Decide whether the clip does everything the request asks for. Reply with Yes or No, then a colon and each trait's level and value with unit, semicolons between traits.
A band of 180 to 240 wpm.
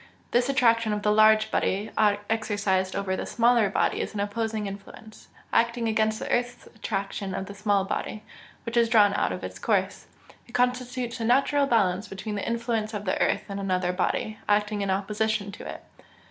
Yes: average, 185 wpm